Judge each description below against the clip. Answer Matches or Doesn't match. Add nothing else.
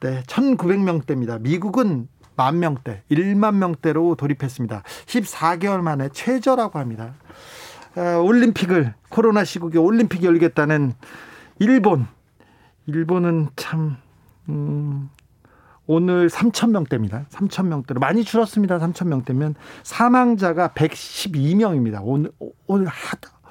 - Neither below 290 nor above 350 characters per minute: Doesn't match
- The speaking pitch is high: Doesn't match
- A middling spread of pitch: Doesn't match